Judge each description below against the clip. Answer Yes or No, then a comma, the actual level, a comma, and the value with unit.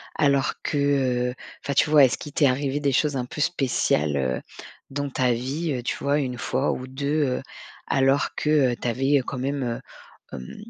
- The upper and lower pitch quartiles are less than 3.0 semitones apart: Yes, narrow, 2.4 semitones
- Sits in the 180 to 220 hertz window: No, low, 135 Hz